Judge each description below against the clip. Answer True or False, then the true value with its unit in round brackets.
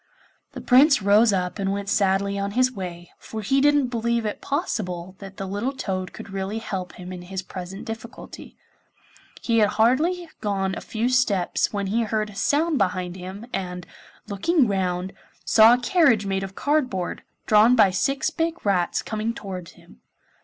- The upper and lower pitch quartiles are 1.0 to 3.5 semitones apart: False (4.1 semitones)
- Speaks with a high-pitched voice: True (205 Hz)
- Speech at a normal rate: True (175 wpm)